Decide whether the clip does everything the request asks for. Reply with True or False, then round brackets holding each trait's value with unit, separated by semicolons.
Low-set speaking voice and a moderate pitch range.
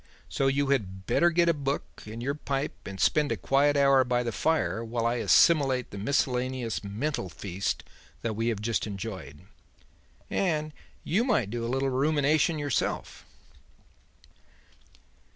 True (130 Hz; 4.3 semitones)